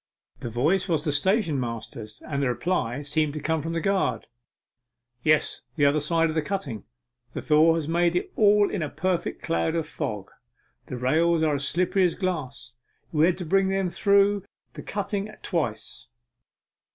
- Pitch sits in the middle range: Yes, medium, 160 Hz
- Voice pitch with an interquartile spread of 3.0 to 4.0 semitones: No, average, 4.5 semitones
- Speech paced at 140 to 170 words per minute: No, average, 180 wpm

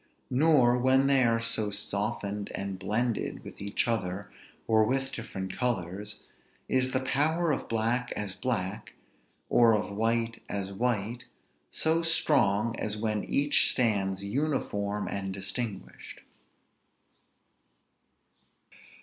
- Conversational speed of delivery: No, slow, 115 wpm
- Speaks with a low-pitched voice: Yes, low, 115 Hz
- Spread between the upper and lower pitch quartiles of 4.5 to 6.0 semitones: No, average, 3.9 semitones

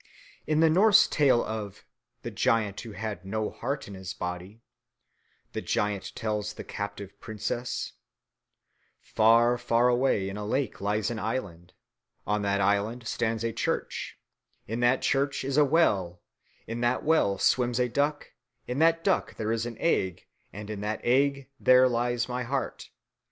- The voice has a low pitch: Yes, low, 115 Hz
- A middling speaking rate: Yes, average, 160 wpm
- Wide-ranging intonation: No, average, 3.9 semitones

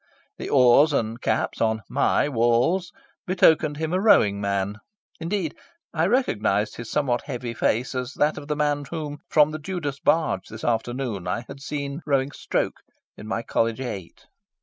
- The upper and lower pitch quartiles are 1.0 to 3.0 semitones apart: No, average, 5.1 semitones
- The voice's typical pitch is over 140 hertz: No, low, 135 Hz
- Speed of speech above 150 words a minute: Yes, average, 165 wpm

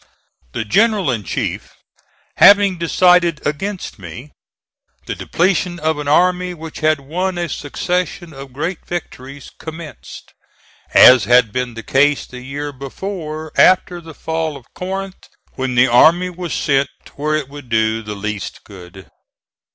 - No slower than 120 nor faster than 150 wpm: Yes, average, 145 wpm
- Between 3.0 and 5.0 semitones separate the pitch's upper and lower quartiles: No, wide, 5.4 semitones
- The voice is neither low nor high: Yes, medium, 150 Hz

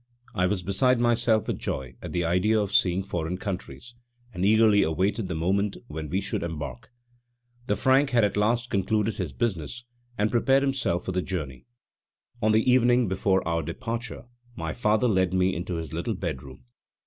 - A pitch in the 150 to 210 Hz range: No, low, 100 Hz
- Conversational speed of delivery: Yes, average, 175 wpm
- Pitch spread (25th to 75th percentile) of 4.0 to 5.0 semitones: Yes, average, 4.6 semitones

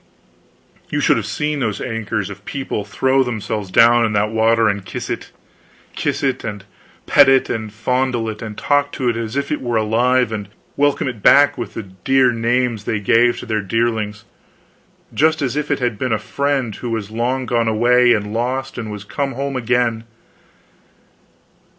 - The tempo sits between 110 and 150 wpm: No, average, 180 wpm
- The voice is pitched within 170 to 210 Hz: No, low, 115 Hz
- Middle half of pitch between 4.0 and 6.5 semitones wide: No, average, 3.2 semitones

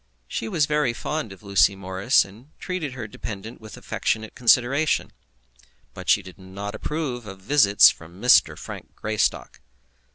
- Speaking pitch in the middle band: No, low, 110 Hz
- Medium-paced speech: Yes, average, 150 wpm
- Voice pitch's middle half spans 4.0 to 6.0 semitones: Yes, wide, 5.4 semitones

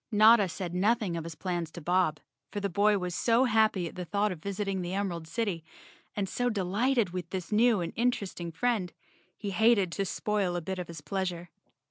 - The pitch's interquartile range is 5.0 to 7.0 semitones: No, average, 3.3 semitones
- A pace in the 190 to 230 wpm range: Yes, average, 200 wpm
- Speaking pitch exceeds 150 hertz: Yes, high, 190 Hz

